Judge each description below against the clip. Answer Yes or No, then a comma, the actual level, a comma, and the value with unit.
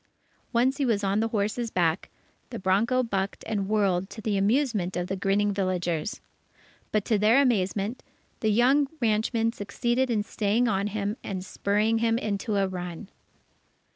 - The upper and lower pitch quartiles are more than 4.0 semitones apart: No, average, 3.0 semitones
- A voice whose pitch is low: No, high, 210 Hz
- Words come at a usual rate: Yes, average, 160 wpm